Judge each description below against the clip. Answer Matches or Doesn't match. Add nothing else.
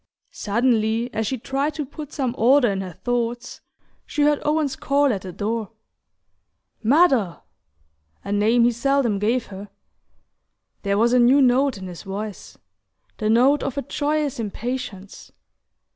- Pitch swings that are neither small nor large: Matches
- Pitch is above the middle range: Matches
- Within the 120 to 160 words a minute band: Matches